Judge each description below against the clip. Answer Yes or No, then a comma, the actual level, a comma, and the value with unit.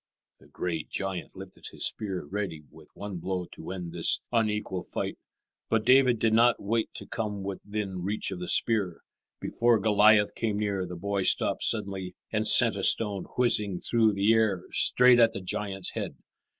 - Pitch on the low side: Yes, low, 100 Hz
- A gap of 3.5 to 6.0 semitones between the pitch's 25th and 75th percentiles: No, average, 2.8 semitones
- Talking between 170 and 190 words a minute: Yes, average, 175 wpm